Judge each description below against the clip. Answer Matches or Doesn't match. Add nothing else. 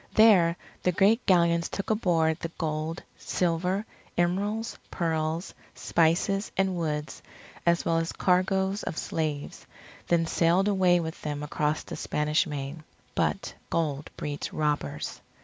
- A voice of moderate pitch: Matches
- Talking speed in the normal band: Doesn't match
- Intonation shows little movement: Doesn't match